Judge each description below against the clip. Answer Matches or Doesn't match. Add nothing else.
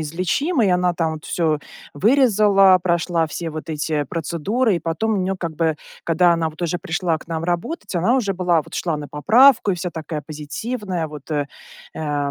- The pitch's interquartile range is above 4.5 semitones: Doesn't match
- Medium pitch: Matches